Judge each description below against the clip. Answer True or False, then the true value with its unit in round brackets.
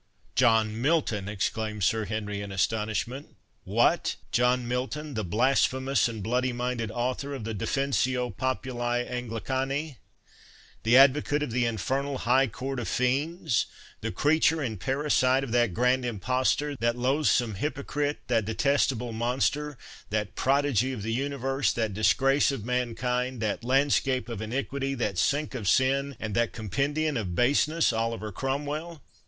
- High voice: False (125 Hz)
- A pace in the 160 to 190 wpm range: False (135 wpm)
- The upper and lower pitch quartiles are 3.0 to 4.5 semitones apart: True (3.4 semitones)